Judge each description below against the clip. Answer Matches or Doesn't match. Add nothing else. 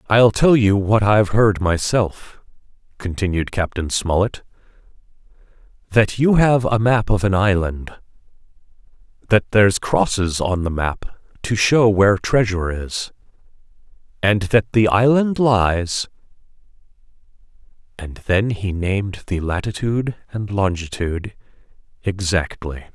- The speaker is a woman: Doesn't match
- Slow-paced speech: Matches